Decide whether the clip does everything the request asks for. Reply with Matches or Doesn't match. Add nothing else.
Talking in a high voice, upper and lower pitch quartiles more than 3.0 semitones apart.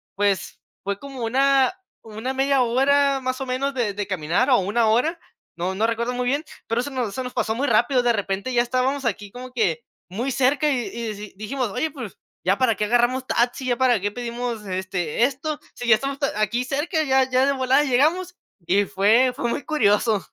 Matches